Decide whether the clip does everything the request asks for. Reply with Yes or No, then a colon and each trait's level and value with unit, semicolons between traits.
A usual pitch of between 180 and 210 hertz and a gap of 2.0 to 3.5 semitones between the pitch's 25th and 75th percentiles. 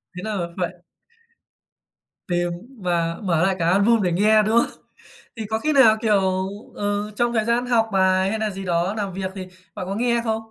Yes: high, 200 Hz; average, 2.9 semitones